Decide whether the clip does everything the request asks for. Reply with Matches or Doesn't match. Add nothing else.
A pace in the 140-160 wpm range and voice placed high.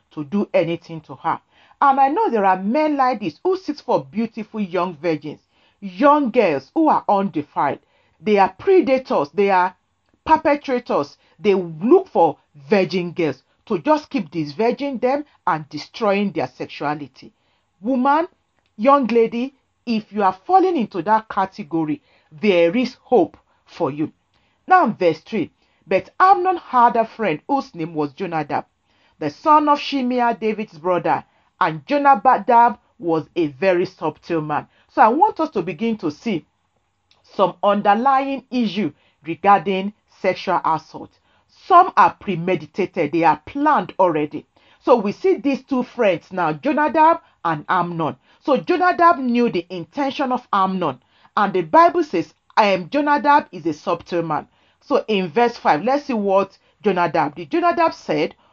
Matches